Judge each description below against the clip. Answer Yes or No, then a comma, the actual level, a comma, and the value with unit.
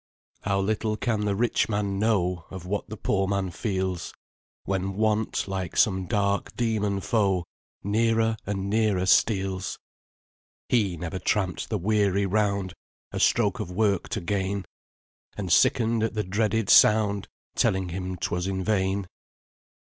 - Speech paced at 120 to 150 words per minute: Yes, average, 140 wpm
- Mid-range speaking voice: No, low, 100 Hz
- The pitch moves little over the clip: Yes, narrow, 2.3 semitones